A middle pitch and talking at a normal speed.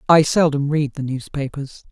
Yes: medium, 145 Hz; average, 155 wpm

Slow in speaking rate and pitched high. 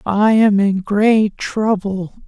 Yes: slow, 130 wpm; high, 205 Hz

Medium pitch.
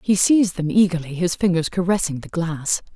Yes: medium, 175 Hz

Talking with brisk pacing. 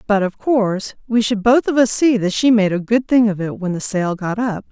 Yes: fast, 280 wpm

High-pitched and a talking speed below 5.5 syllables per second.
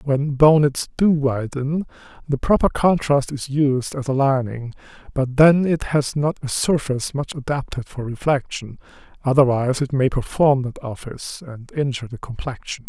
No: low, 135 Hz; 4.7 syllables/s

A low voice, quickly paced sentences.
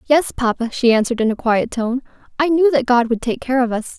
No: very high, 250 Hz; fast, 255 wpm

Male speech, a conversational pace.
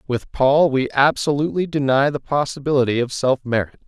Yes: male; average, 155 wpm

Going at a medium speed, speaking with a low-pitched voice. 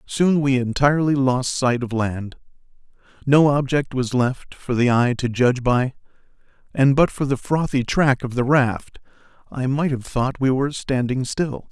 Yes: average, 175 wpm; low, 130 Hz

